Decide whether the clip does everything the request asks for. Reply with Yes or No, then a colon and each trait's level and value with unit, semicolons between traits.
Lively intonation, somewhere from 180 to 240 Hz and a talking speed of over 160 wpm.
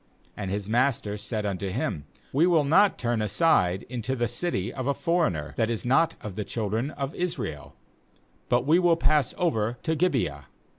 No: wide, 6.8 semitones; low, 120 Hz; average, 180 wpm